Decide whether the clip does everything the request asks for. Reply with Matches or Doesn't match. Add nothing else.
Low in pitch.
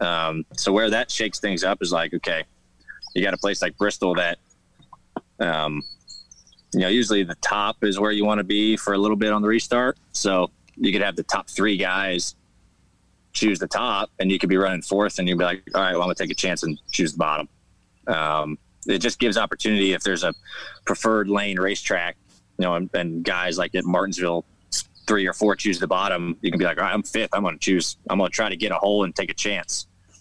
Matches